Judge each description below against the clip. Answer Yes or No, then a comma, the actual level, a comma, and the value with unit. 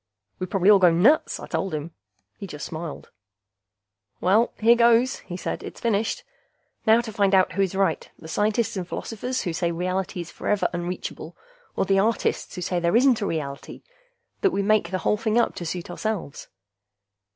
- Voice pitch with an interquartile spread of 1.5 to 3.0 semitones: No, average, 4.0 semitones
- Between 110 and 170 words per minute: No, average, 185 wpm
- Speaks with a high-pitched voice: Yes, high, 195 Hz